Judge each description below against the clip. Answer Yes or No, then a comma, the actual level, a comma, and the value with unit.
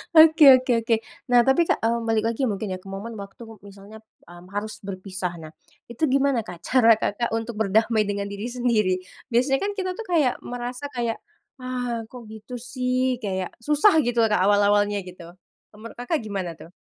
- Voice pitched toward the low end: No, high, 225 Hz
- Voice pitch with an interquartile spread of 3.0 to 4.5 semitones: Yes, average, 3.8 semitones